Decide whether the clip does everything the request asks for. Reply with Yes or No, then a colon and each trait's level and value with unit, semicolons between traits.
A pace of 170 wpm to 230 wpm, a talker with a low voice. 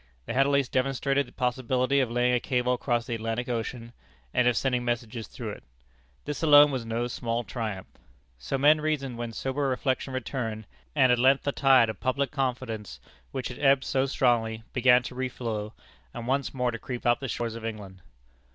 Yes: average, 195 wpm; low, 125 Hz